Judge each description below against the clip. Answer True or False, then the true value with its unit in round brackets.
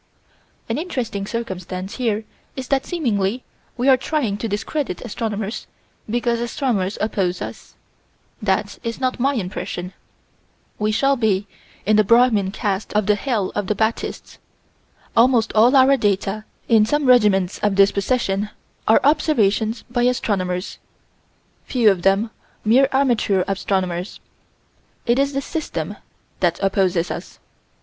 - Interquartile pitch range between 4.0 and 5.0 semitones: True (4.3 semitones)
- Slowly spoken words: True (130 wpm)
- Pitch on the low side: False (215 Hz)